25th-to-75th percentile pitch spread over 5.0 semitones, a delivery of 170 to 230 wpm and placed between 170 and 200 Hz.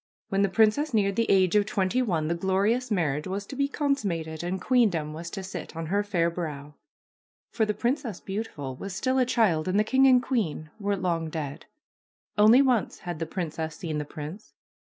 Yes: wide, 5.4 semitones; average, 195 wpm; high, 190 Hz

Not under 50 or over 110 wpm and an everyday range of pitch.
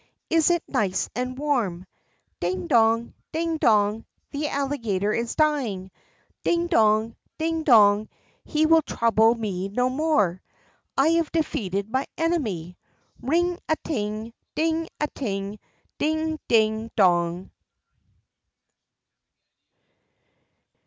No: slow, 105 wpm; wide, 7.1 semitones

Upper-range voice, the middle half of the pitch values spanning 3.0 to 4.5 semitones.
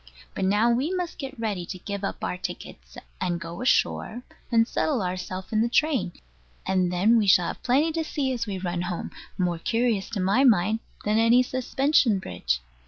No: high, 215 Hz; average, 5.2 semitones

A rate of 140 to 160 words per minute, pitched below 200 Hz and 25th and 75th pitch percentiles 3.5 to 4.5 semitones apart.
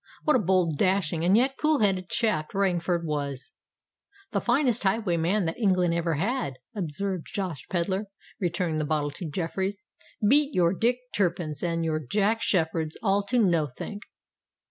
Yes: average, 150 wpm; medium, 185 Hz; average, 4.1 semitones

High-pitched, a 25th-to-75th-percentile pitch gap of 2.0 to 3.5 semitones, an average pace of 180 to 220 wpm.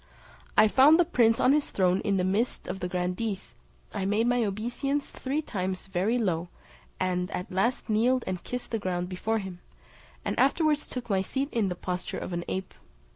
No: high, 205 Hz; average, 5.1 semitones; average, 190 wpm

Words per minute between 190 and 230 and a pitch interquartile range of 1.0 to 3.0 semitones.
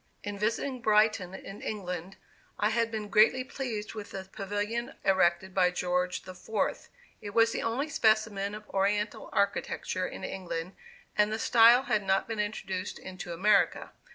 No: average, 155 wpm; average, 2.7 semitones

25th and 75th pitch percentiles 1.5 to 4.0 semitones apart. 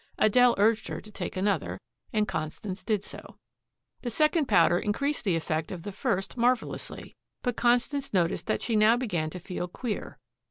No: average, 5.0 semitones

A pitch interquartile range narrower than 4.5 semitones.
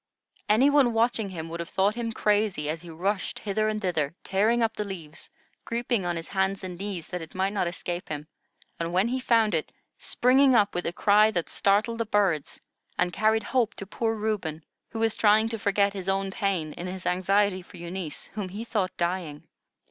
Yes: average, 3.6 semitones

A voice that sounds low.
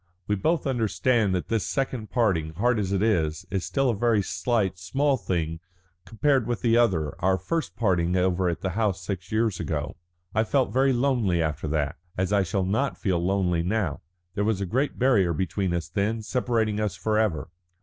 Yes: low, 100 Hz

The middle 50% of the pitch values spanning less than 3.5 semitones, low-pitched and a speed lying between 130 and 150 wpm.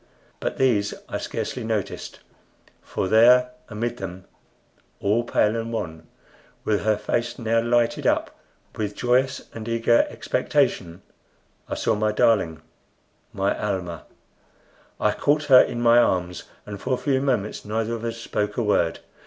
Yes: average, 2.8 semitones; low, 110 Hz; average, 145 wpm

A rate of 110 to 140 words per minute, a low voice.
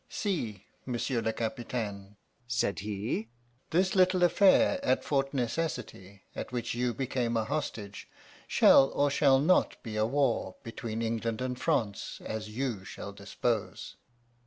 Yes: slow, 135 wpm; low, 120 Hz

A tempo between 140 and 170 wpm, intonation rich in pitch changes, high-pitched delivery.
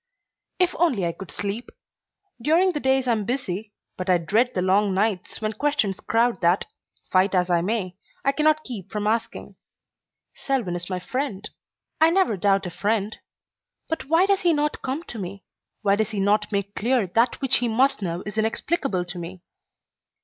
No: average, 185 wpm; wide, 5.8 semitones; high, 215 Hz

